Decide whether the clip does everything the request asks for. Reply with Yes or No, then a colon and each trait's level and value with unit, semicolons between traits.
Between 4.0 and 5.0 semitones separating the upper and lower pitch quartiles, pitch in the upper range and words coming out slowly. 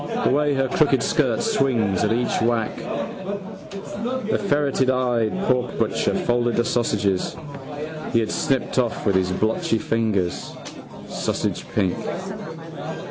No: average, 4.3 semitones; low, 120 Hz; slow, 105 wpm